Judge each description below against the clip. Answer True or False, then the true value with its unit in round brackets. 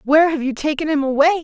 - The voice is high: True (295 Hz)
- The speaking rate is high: True (250 wpm)